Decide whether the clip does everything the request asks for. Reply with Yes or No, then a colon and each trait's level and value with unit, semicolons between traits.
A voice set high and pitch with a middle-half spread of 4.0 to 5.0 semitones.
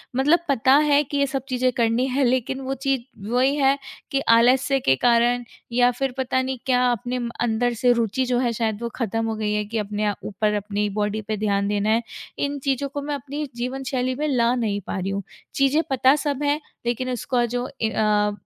No: high, 245 Hz; average, 3.5 semitones